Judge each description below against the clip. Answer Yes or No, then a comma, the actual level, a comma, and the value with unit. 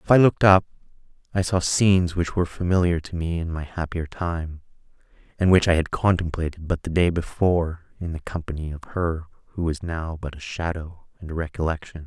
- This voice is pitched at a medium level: No, very low, 85 Hz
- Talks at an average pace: Yes, average, 195 wpm